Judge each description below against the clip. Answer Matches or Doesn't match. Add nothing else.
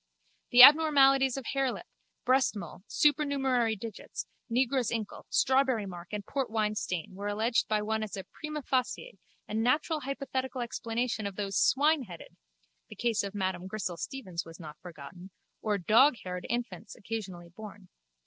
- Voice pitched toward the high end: Matches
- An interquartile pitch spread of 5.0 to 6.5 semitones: Matches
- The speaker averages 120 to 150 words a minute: Matches